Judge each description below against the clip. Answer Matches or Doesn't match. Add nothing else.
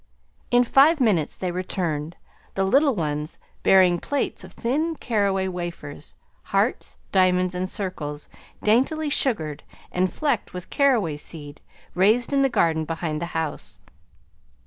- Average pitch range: Doesn't match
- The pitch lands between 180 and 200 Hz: Matches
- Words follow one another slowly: Matches